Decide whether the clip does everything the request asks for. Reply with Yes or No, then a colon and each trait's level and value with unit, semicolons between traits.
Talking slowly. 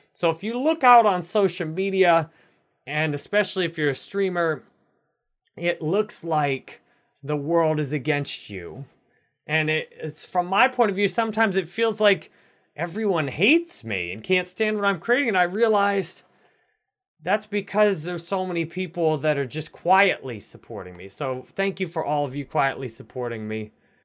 No: average, 170 wpm